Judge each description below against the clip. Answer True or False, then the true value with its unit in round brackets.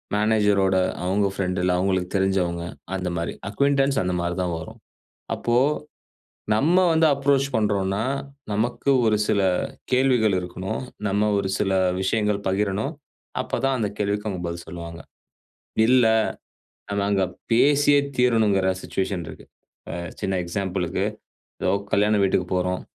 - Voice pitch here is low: True (100 Hz)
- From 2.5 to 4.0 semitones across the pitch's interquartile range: True (3.3 semitones)